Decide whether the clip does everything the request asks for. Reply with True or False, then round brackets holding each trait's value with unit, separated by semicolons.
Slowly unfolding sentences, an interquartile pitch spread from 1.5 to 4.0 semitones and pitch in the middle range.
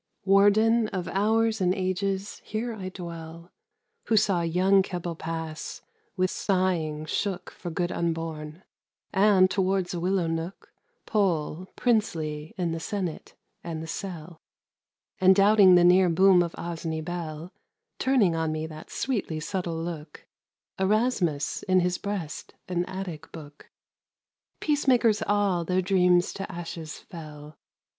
True (130 wpm; 3.1 semitones; 180 Hz)